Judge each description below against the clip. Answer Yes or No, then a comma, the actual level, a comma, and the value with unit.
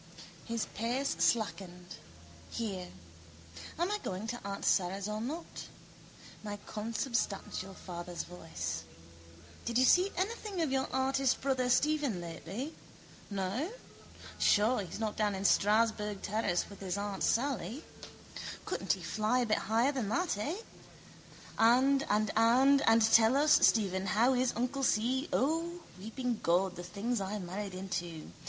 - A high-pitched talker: Yes, high, 220 Hz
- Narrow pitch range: No, average, 5.1 semitones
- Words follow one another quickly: No, average, 140 wpm